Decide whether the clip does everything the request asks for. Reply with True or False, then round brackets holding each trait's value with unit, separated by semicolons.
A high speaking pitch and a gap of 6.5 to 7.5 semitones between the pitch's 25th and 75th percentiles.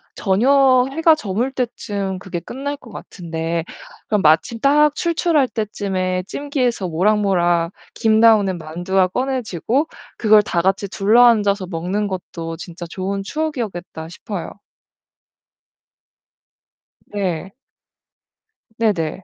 False (200 Hz; 5.2 semitones)